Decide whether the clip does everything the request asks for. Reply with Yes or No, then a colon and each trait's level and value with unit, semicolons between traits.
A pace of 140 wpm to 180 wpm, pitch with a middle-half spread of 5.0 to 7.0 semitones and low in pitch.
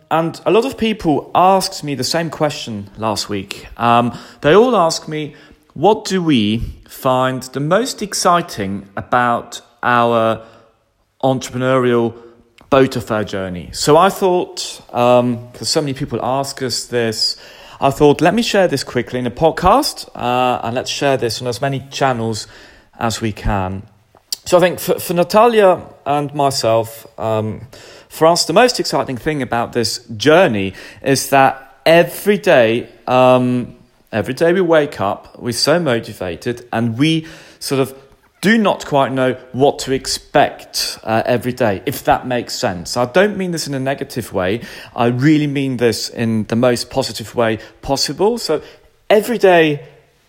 Yes: average, 160 wpm; wide, 5.4 semitones; low, 130 Hz